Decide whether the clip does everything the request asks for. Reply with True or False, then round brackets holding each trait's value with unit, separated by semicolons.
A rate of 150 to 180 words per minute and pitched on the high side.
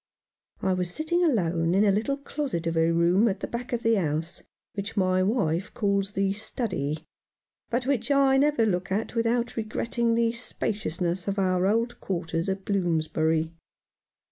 True (165 wpm; 200 Hz)